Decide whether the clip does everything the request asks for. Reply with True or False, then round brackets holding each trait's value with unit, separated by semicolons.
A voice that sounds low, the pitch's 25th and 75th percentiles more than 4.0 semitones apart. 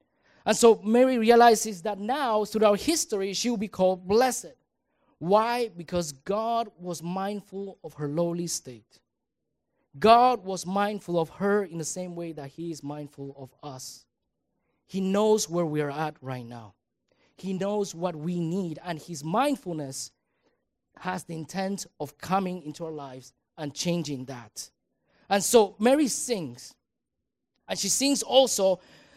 False (185 Hz; 5.3 semitones)